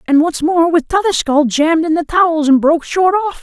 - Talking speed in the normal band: No, fast, 230 wpm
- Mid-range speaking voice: No, very high, 325 Hz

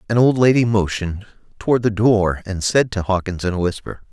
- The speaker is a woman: No, male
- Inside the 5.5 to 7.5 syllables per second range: Yes, 5.7 syllables/s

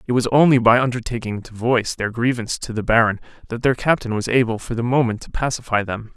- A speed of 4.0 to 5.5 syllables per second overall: No, 6.4 syllables/s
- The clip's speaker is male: Yes, male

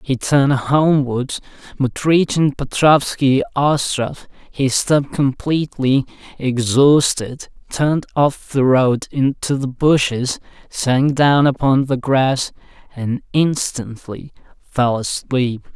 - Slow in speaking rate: Yes, slow, 105 wpm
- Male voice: Yes, male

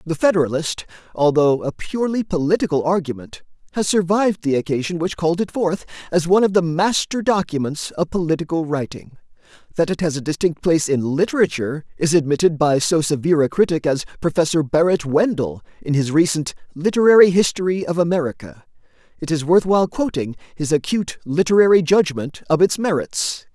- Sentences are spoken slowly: No, average, 160 wpm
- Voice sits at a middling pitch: Yes, medium, 165 Hz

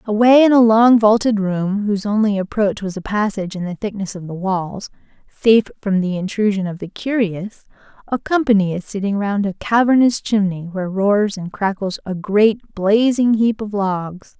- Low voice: No, high, 205 Hz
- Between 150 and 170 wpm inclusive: No, average, 180 wpm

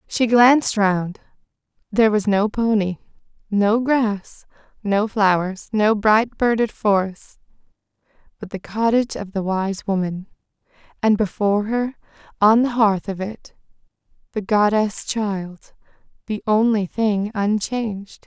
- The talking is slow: Yes, slow, 115 wpm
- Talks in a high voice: Yes, high, 210 Hz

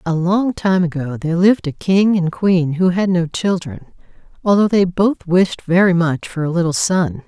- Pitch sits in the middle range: Yes, medium, 175 Hz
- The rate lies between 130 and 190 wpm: No, average, 200 wpm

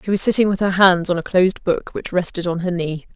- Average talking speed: No, fast, 285 wpm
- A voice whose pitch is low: No, medium, 180 Hz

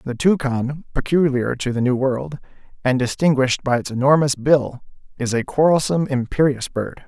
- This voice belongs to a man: Yes, male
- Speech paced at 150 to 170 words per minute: Yes, average, 155 wpm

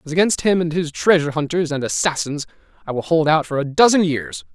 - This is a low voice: No, medium, 155 Hz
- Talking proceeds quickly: Yes, fast, 225 wpm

